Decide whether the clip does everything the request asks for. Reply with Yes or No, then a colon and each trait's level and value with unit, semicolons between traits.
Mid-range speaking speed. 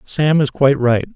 No: fast, 210 wpm